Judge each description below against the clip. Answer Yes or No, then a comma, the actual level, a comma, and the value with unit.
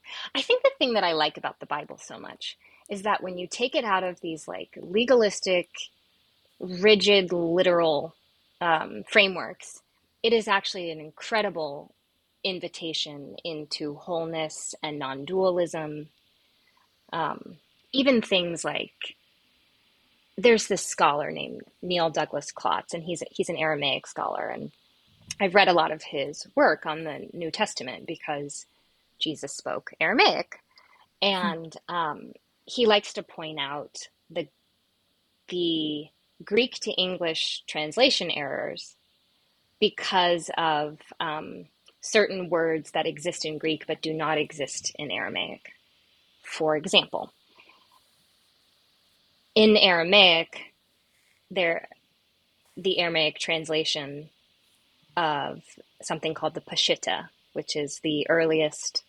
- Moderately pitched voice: Yes, medium, 170 Hz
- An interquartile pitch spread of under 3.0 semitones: No, average, 4.2 semitones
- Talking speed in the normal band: No, slow, 120 wpm